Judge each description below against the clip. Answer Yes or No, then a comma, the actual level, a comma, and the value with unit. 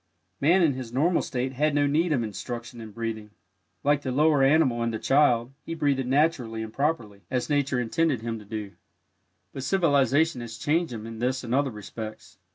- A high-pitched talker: No, low, 130 Hz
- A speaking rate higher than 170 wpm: Yes, average, 190 wpm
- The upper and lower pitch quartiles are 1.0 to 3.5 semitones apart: No, average, 4.2 semitones